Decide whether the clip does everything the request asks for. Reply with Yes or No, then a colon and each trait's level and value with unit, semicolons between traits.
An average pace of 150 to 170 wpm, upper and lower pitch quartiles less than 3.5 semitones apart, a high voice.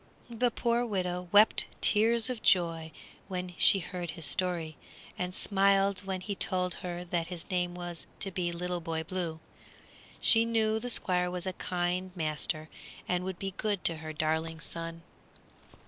No: average, 165 wpm; narrow, 2.5 semitones; medium, 180 Hz